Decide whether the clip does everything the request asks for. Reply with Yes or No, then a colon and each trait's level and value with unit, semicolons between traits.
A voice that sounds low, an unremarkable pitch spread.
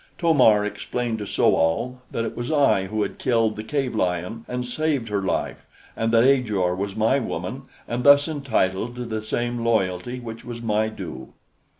Yes: low, 115 Hz; average, 3.2 semitones